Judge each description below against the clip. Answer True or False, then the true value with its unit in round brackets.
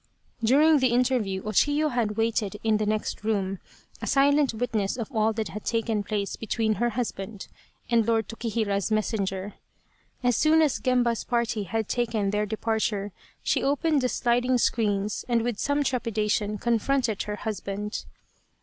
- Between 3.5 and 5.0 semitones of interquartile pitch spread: False (2.8 semitones)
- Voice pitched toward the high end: True (225 Hz)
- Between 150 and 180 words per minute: True (160 wpm)